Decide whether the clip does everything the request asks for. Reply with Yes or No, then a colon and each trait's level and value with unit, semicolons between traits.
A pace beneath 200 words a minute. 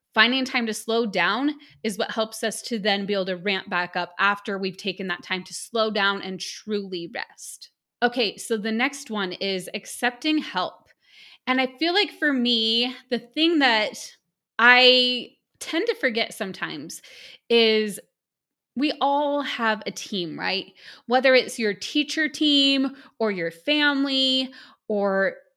Yes: average, 155 wpm